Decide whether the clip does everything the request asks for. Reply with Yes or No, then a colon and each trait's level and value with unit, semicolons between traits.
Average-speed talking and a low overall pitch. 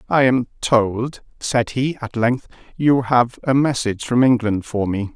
Yes: average, 175 wpm; low, 120 Hz